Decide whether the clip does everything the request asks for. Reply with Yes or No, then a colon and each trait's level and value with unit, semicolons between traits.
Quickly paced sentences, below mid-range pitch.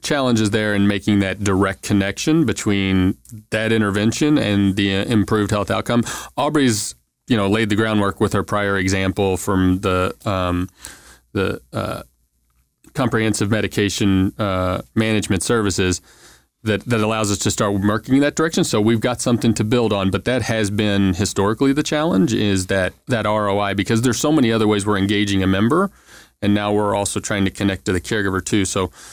No: average, 175 wpm; low, 105 Hz